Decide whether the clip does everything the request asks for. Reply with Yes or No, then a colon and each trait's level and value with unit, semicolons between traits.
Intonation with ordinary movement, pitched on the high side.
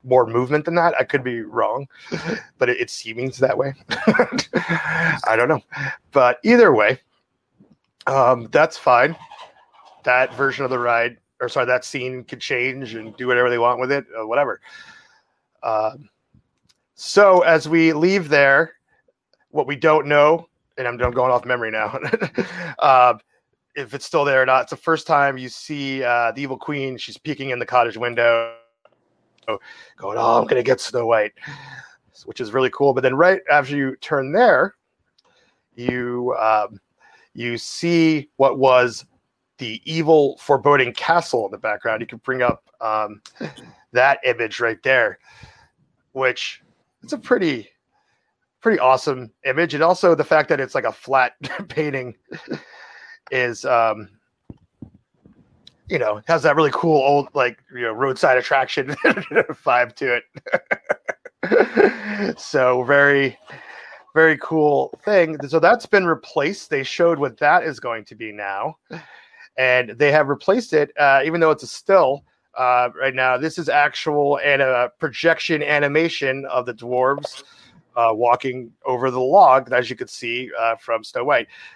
No: average, 3.9 semitones; low, 135 Hz